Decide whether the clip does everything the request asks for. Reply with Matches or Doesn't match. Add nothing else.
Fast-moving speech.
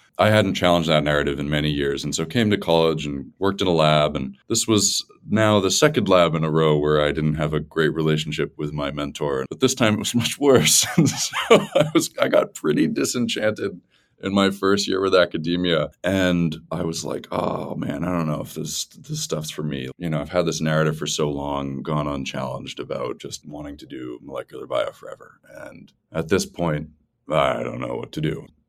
Matches